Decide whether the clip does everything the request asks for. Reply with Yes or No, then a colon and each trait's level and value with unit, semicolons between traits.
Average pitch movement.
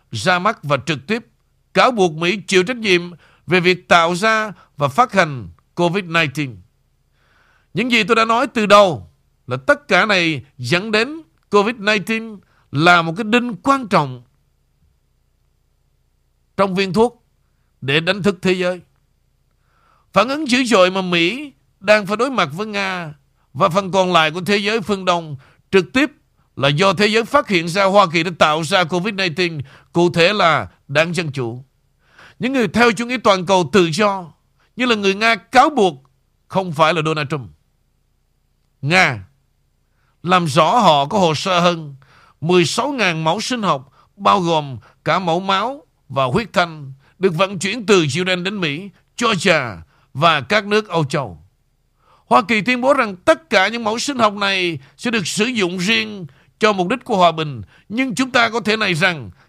No: wide, 5.8 semitones